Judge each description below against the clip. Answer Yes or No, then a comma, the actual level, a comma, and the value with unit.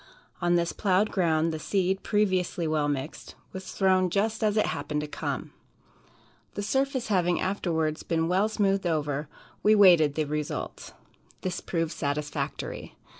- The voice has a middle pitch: Yes, medium, 175 Hz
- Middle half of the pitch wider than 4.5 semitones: No, average, 4.1 semitones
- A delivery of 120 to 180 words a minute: Yes, average, 145 wpm